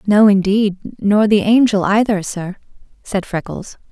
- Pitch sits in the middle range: No, high, 205 Hz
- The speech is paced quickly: No, average, 140 wpm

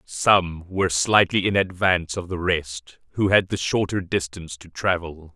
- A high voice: No, very low, 90 Hz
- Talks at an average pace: Yes, average, 170 wpm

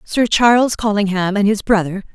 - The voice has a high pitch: Yes, high, 210 Hz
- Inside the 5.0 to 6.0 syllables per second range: Yes, 5.1 syllables/s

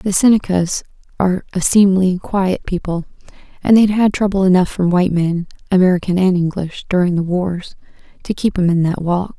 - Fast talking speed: No, average, 160 wpm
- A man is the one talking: No, female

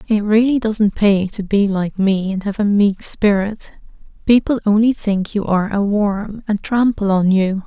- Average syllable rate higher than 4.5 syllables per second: No, 4.4 syllables/s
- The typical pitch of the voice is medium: No, high, 205 Hz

